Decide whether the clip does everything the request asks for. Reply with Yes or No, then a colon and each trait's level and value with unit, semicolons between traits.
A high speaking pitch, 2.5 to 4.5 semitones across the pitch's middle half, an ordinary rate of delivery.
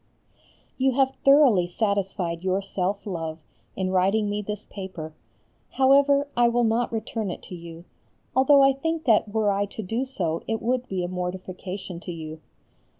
No: high, 205 Hz; average, 5.1 semitones; average, 165 wpm